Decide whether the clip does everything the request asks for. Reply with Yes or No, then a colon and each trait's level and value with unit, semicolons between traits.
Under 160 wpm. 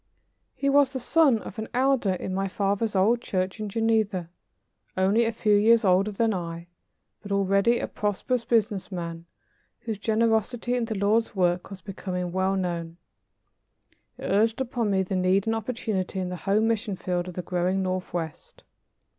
No: average, 170 wpm